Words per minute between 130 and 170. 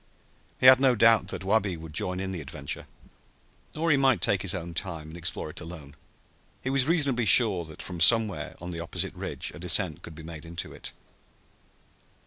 No: average, 195 wpm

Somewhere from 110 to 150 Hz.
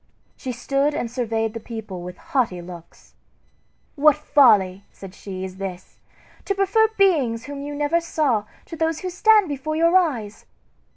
No: very high, 265 Hz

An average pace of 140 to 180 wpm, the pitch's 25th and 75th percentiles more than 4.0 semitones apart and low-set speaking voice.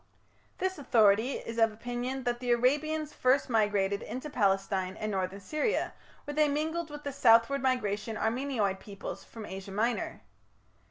No: average, 150 wpm; average, 5.3 semitones; high, 240 Hz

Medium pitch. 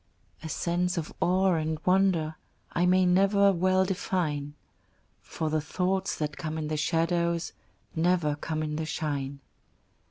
Yes: medium, 170 Hz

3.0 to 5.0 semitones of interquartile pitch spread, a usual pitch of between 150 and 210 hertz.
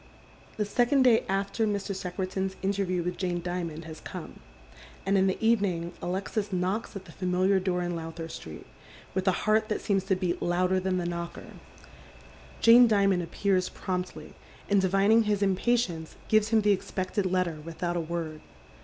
No: narrow, 2.5 semitones; high, 190 Hz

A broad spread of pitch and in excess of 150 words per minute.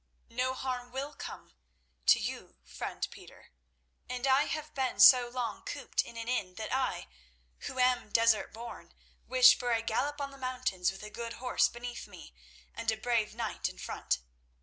No: average, 2.8 semitones; average, 170 wpm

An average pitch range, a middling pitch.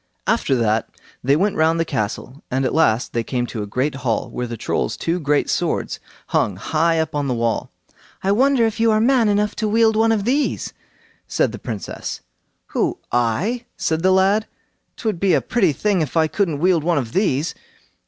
No: wide, 8.4 semitones; medium, 165 Hz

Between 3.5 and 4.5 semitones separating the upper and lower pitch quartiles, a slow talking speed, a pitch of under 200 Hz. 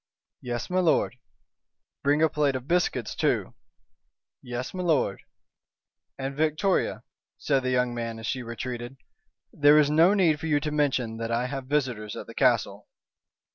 No: average, 3.9 semitones; average, 150 wpm; low, 135 Hz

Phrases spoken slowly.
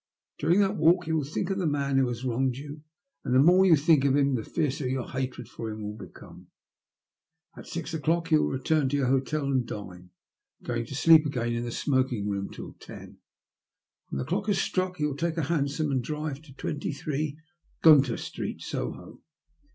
No: fast, 205 wpm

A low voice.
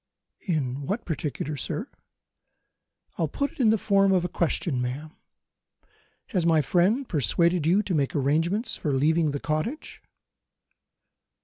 No: medium, 165 Hz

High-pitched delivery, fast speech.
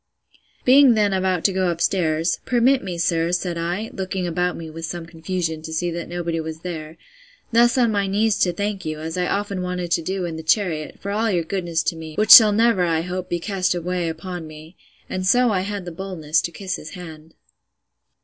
No: medium, 180 Hz; fast, 215 wpm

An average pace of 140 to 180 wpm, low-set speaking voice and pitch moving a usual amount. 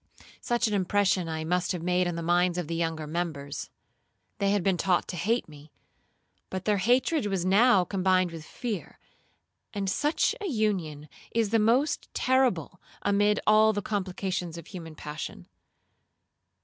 No: average, 160 wpm; medium, 185 Hz; average, 3.8 semitones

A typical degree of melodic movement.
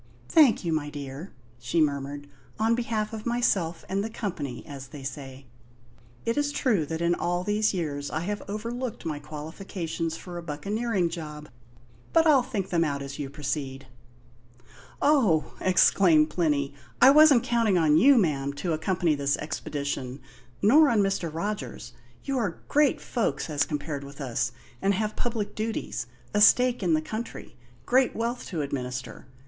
No: wide, 7.1 semitones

